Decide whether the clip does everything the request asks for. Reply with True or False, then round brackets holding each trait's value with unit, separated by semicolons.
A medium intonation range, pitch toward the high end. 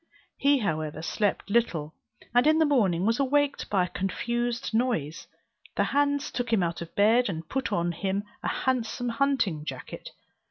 False (6.9 semitones; 225 Hz)